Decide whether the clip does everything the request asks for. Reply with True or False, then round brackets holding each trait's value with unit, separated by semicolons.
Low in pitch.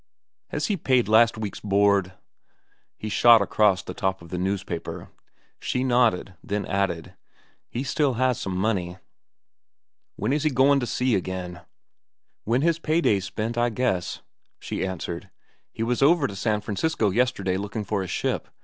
True (105 Hz)